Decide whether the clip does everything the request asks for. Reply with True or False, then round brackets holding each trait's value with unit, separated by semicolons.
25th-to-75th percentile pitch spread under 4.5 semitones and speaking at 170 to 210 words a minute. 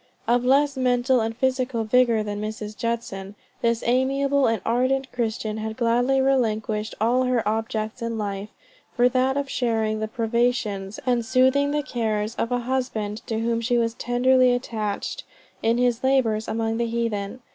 False (2.6 semitones; 160 wpm)